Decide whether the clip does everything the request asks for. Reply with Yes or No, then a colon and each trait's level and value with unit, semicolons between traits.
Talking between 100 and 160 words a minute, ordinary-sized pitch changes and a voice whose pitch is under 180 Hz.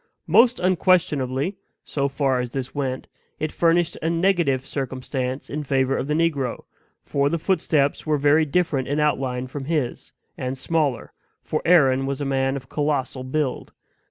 Yes: average, 155 wpm; average, 3.4 semitones; medium, 140 Hz